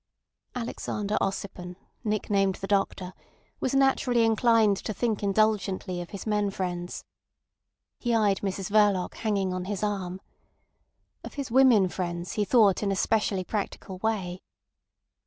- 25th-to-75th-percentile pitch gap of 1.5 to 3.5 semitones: Yes, average, 2.7 semitones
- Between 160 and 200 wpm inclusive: No, slow, 135 wpm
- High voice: Yes, high, 200 Hz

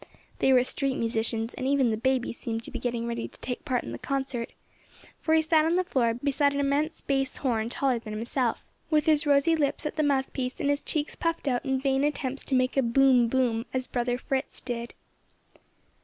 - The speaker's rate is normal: No, fast, 215 wpm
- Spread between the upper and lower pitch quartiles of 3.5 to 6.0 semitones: No, average, 3.0 semitones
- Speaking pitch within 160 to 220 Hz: No, very high, 265 Hz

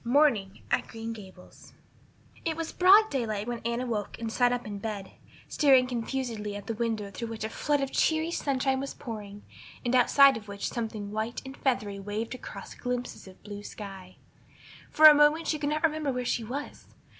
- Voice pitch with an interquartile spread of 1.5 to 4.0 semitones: No, average, 4.7 semitones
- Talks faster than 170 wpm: Yes, average, 190 wpm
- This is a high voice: Yes, high, 235 Hz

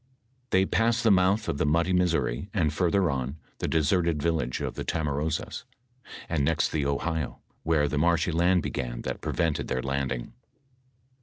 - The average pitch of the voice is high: No, very low, 80 Hz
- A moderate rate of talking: Yes, average, 160 wpm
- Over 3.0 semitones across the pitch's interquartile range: Yes, average, 3.9 semitones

